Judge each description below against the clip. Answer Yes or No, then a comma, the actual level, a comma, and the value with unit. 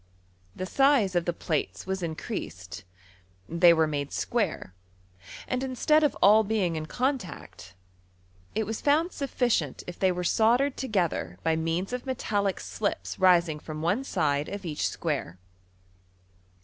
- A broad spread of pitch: Yes, wide, 6.8 semitones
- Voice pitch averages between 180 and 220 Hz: Yes, medium, 185 Hz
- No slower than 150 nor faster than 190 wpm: No, average, 140 wpm